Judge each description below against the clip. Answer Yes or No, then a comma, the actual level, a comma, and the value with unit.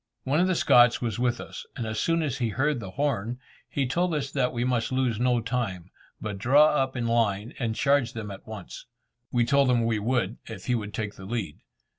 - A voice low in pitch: Yes, low, 120 Hz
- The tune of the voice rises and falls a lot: No, average, 3.4 semitones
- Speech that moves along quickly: Yes, fast, 225 wpm